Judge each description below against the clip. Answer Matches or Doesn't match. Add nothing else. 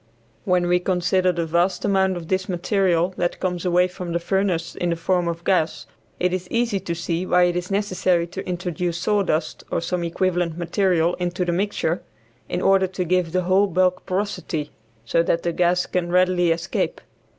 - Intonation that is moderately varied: Doesn't match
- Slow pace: Doesn't match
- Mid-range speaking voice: Matches